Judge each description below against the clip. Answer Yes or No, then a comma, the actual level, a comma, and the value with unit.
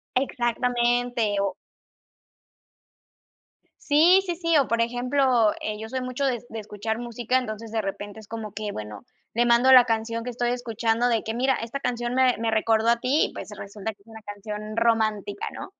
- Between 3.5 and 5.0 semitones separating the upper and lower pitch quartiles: No, narrow, 2.4 semitones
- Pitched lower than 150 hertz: No, high, 230 Hz